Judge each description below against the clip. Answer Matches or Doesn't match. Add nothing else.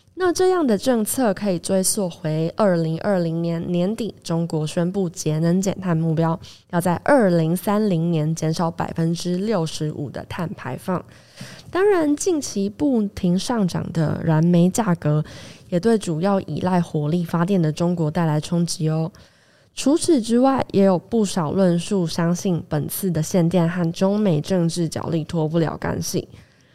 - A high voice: Doesn't match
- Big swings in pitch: Doesn't match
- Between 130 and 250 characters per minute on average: Matches